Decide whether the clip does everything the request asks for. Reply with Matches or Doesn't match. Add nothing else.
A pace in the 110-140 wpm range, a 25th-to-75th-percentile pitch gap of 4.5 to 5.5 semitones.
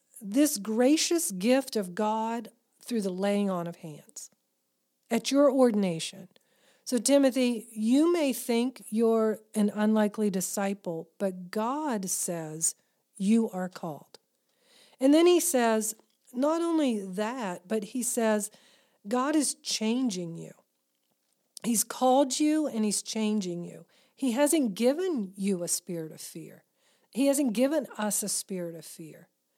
Matches